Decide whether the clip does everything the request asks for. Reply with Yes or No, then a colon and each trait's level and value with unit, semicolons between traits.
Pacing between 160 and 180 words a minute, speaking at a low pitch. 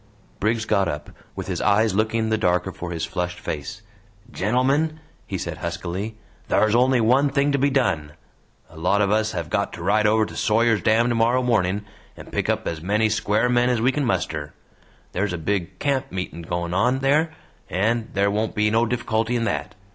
No: average, 195 wpm; low, 110 Hz